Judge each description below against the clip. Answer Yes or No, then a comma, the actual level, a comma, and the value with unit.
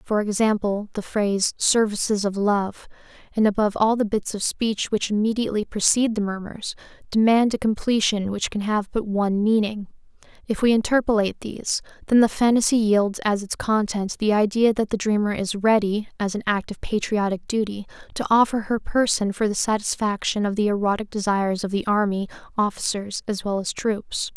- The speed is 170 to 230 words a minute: Yes, average, 175 wpm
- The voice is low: No, high, 210 Hz